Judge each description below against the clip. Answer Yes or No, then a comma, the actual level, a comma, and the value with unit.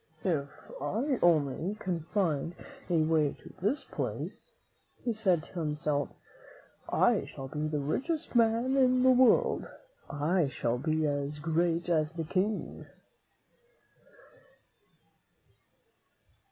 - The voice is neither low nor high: Yes, medium, 165 Hz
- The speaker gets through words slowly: Yes, slow, 115 wpm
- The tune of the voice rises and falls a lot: Yes, wide, 6.0 semitones